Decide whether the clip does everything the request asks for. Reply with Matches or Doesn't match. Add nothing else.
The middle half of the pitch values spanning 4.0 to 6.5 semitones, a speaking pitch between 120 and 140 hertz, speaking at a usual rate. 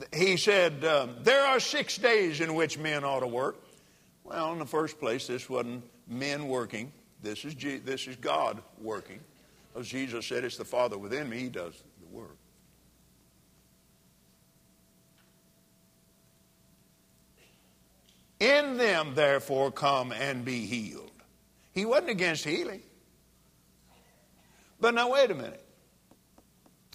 Doesn't match